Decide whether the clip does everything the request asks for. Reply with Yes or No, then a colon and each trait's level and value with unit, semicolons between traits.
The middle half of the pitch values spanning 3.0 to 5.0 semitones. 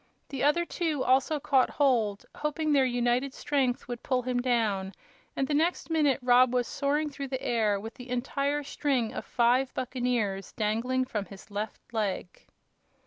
Yes: average, 3.3 semitones